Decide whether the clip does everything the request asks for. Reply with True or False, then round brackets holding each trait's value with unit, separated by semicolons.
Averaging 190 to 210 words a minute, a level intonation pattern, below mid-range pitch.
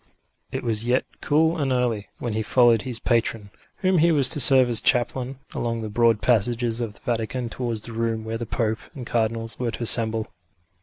True (200 wpm; 1.9 semitones; 115 Hz)